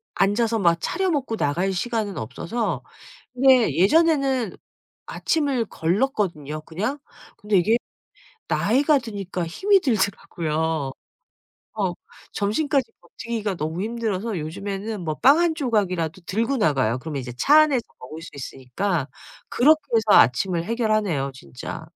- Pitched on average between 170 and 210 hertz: Yes, high, 205 Hz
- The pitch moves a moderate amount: No, wide, 6.8 semitones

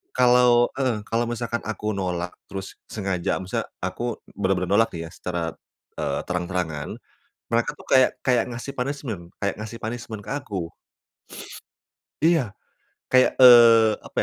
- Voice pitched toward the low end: Yes, low, 110 Hz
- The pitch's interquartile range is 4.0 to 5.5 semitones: Yes, average, 4.6 semitones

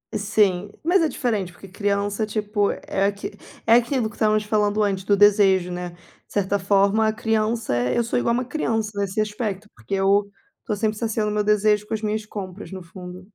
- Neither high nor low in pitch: No, high, 210 Hz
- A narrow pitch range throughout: Yes, narrow, 1.8 semitones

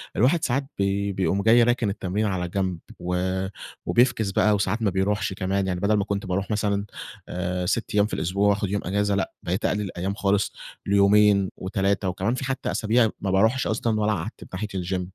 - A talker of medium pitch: No, low, 100 Hz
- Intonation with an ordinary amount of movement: No, narrow, 2.1 semitones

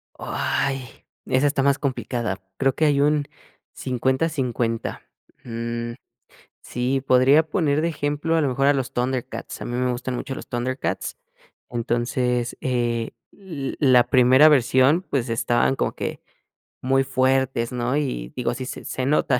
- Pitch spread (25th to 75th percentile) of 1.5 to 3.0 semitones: Yes, narrow, 2.5 semitones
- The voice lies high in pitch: No, low, 130 Hz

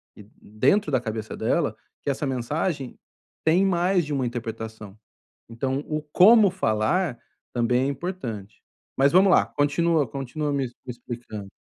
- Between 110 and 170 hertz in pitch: Yes, low, 135 Hz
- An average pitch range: No, wide, 6.0 semitones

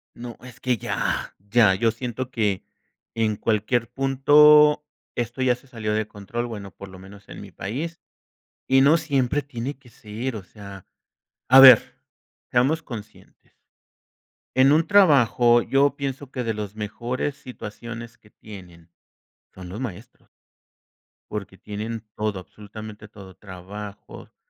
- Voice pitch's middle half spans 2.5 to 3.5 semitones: No, average, 4.0 semitones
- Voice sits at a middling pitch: No, low, 115 Hz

